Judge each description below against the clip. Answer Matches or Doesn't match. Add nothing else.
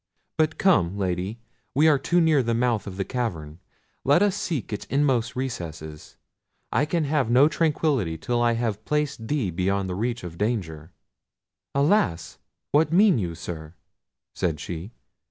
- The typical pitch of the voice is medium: Doesn't match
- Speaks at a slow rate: Doesn't match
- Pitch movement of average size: Doesn't match